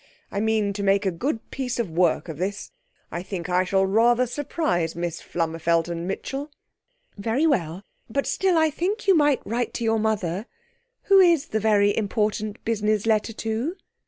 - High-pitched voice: Yes, high, 215 Hz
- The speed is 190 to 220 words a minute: No, average, 175 wpm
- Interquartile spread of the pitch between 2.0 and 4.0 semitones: No, average, 5.3 semitones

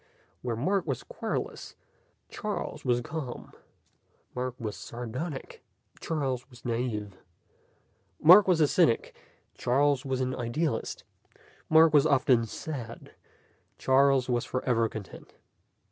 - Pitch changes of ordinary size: Yes, average, 3.7 semitones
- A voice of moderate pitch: No, low, 130 Hz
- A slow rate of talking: Yes, slow, 110 wpm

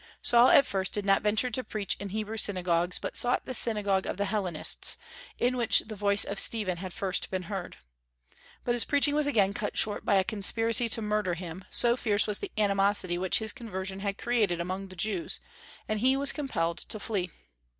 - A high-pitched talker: Yes, high, 205 Hz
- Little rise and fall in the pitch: No, average, 3.2 semitones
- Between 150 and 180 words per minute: No, average, 200 wpm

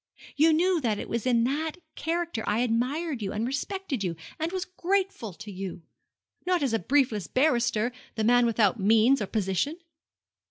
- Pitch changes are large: Yes, wide, 6.6 semitones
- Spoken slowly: No, average, 170 wpm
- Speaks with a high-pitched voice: Yes, high, 245 Hz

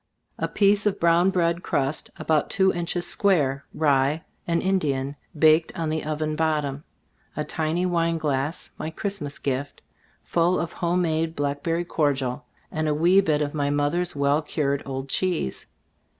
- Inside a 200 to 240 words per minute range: No, average, 155 wpm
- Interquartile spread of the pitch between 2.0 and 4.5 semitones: Yes, average, 3.1 semitones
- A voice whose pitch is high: No, medium, 155 Hz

